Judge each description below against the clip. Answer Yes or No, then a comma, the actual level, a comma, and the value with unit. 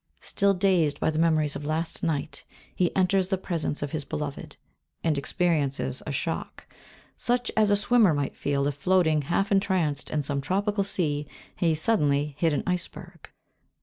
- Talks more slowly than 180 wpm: Yes, average, 170 wpm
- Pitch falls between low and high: Yes, medium, 160 Hz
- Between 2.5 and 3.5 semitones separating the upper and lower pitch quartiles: No, average, 4.4 semitones